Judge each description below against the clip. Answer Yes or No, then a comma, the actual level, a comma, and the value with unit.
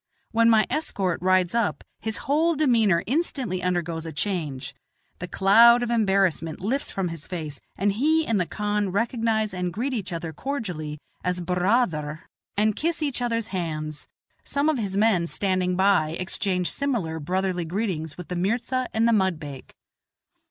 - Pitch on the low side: No, high, 195 Hz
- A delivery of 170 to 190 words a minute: No, average, 160 wpm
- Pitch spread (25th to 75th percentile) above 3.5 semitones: Yes, average, 4.8 semitones